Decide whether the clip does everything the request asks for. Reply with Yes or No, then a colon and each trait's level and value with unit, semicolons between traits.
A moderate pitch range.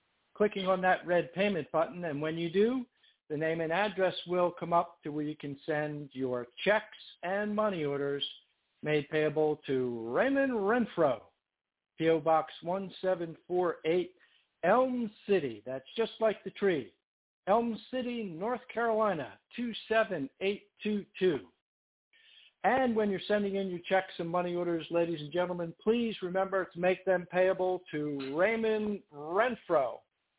Yes: average, 4.7 semitones